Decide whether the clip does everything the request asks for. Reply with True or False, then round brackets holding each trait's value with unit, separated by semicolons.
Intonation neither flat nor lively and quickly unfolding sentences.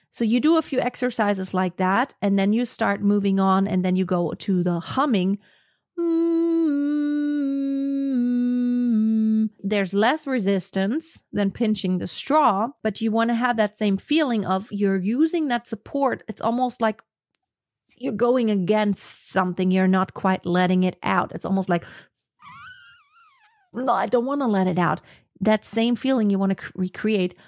False (4.7 semitones; 160 wpm)